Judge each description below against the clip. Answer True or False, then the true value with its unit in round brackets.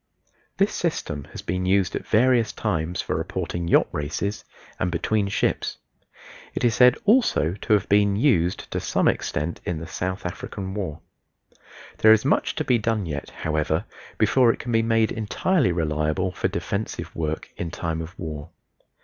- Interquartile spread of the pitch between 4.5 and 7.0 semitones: True (5.1 semitones)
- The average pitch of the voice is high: False (95 Hz)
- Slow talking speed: False (165 wpm)